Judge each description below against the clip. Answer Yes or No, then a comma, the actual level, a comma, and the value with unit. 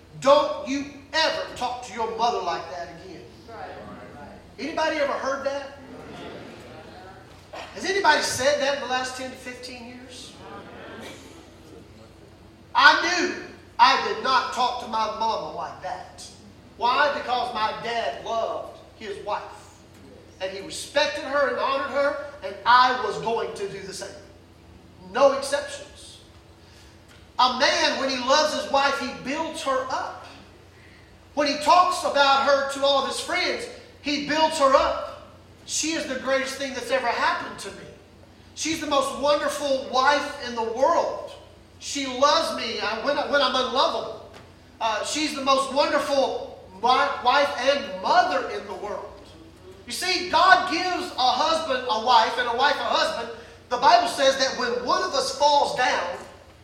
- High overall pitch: Yes, very high, 275 Hz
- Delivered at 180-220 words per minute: No, average, 155 wpm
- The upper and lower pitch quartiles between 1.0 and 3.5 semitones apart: Yes, average, 3.1 semitones